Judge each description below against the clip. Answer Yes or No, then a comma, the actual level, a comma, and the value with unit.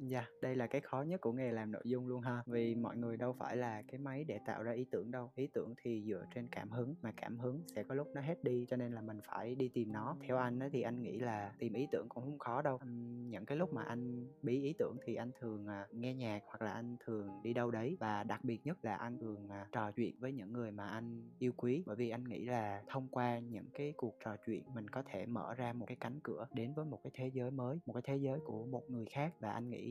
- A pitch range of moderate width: No, narrow, 2.2 semitones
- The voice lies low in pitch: Yes, low, 120 Hz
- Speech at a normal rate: No, fast, 285 wpm